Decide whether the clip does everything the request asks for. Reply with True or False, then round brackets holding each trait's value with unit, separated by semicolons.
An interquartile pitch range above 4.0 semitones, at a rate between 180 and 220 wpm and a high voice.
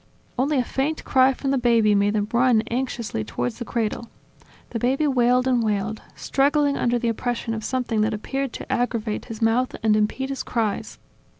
False (3.1 semitones; 185 wpm; 240 Hz)